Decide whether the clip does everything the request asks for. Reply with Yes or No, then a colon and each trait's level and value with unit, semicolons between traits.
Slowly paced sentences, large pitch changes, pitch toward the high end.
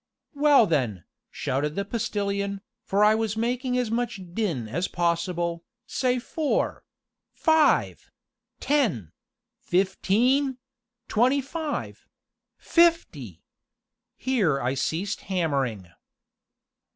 Yes: slow, 90 wpm; wide, 7.3 semitones; high, 200 Hz